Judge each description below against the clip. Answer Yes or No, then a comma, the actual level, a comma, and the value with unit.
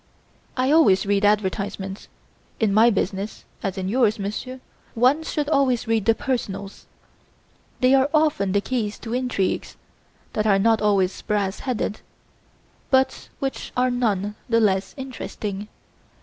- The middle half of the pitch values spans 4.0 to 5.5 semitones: Yes, average, 4.3 semitones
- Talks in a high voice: Yes, high, 215 Hz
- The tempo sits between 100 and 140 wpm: Yes, slow, 135 wpm